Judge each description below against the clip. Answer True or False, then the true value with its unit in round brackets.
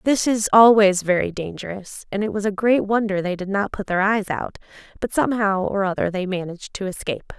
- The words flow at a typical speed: False (210 wpm)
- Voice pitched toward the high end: True (200 Hz)